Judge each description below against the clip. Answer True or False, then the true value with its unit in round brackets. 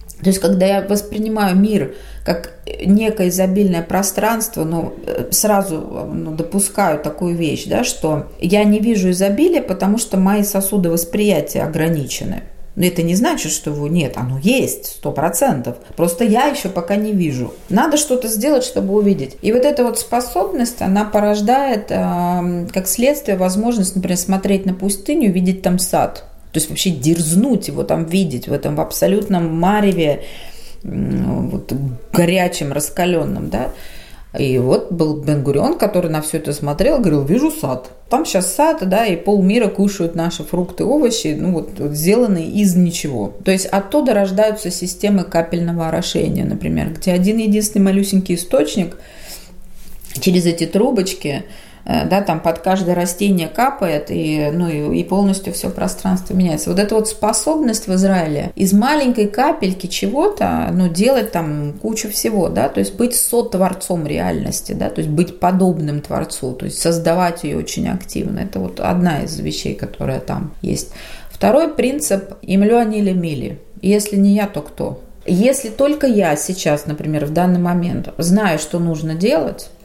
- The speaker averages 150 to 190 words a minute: True (155 wpm)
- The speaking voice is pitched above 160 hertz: True (190 Hz)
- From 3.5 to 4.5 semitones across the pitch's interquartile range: True (3.8 semitones)